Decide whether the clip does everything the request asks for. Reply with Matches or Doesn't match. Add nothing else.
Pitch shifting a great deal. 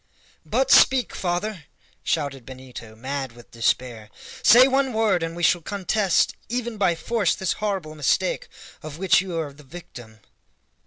Matches